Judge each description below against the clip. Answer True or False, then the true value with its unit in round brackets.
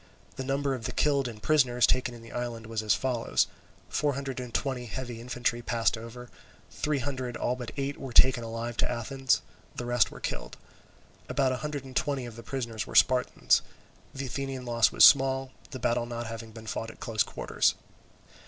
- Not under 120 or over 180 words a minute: False (200 wpm)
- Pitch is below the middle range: True (125 Hz)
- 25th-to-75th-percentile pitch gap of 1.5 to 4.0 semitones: True (2.4 semitones)